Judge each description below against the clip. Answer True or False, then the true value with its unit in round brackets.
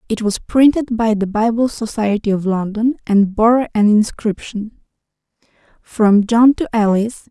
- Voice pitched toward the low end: False (220 Hz)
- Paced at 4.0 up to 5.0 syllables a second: True (4.4 syllables/s)